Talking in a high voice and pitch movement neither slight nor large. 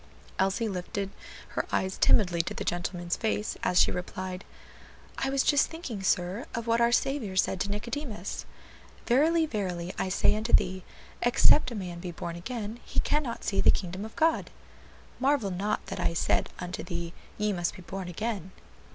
Yes: high, 200 Hz; average, 4.7 semitones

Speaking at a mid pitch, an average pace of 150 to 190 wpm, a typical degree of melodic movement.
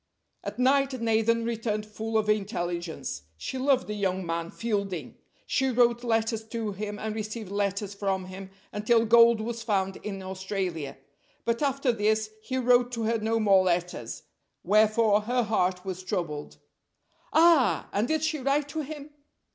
No: high, 215 Hz; average, 155 wpm; average, 3.5 semitones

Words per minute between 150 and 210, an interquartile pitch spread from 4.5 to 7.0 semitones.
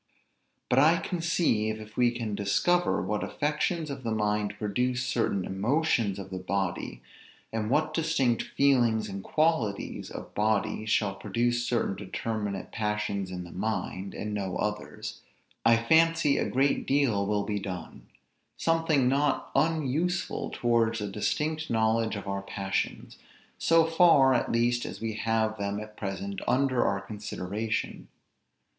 No: average, 140 wpm; average, 5.1 semitones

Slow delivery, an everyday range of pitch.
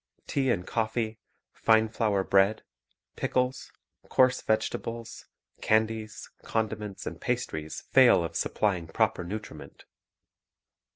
No: slow, 105 wpm; narrow, 1.8 semitones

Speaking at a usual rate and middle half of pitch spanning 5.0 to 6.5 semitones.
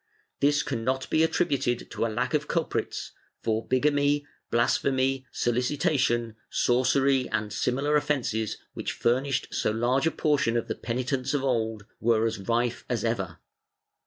No: average, 150 wpm; average, 3.3 semitones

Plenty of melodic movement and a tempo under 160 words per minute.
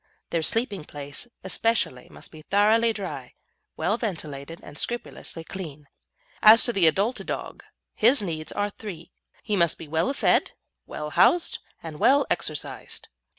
Yes: wide, 6.1 semitones; average, 145 wpm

